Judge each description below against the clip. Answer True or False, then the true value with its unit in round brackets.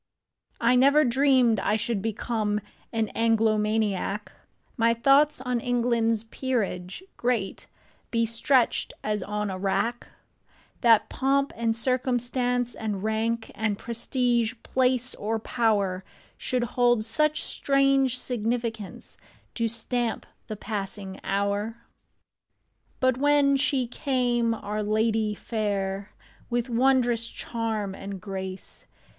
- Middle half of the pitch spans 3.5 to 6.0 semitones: False (2.9 semitones)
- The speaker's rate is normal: False (105 wpm)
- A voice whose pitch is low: False (230 Hz)